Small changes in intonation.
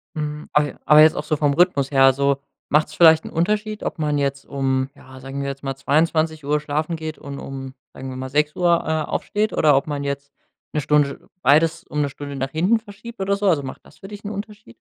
No: average, 3.1 semitones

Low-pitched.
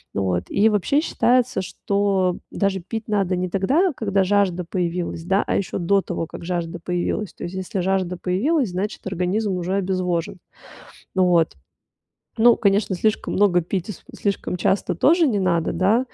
No: high, 190 Hz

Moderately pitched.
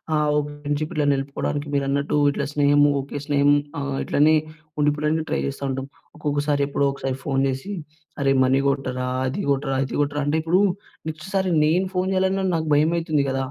Yes: medium, 145 Hz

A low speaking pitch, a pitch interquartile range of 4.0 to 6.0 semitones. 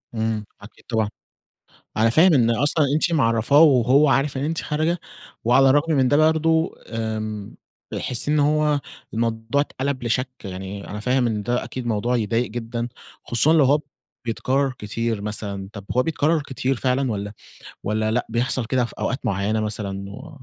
Yes: low, 120 Hz; average, 4.6 semitones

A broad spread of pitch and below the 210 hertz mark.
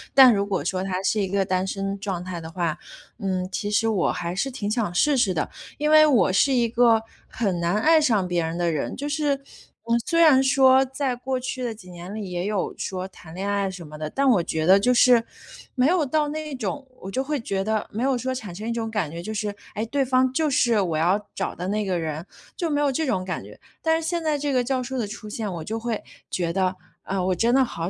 No: wide, 6.1 semitones; high, 215 Hz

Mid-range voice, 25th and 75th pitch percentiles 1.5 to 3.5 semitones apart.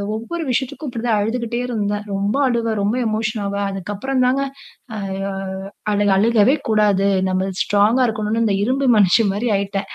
No: high, 215 Hz; average, 2.9 semitones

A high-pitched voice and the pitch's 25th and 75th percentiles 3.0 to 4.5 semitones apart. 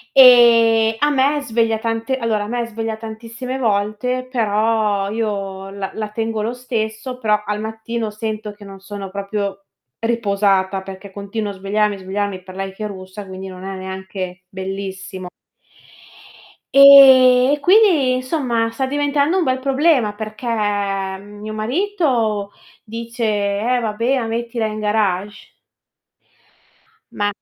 Yes: high, 220 Hz; average, 3.4 semitones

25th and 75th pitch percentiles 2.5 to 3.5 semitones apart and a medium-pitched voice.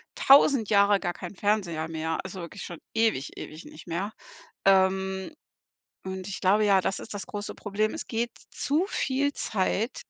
No: average, 2.8 semitones; high, 195 Hz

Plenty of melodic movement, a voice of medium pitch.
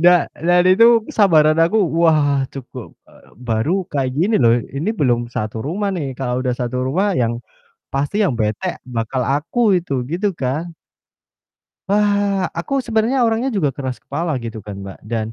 Yes: wide, 7.6 semitones; medium, 155 Hz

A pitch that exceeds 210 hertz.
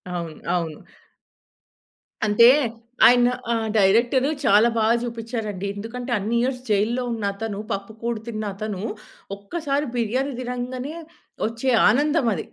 Yes: high, 230 Hz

